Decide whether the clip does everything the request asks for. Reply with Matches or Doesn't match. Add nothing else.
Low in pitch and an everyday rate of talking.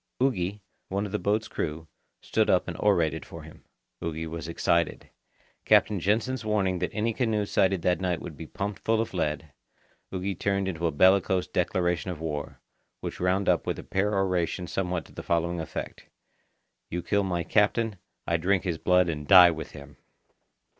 Matches